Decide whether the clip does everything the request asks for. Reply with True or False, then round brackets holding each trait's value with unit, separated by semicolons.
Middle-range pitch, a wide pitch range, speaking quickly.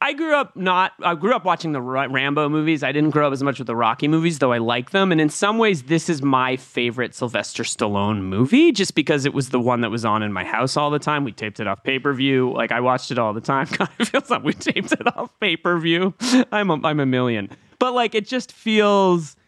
True (150 Hz; 7.0 semitones; 260 wpm)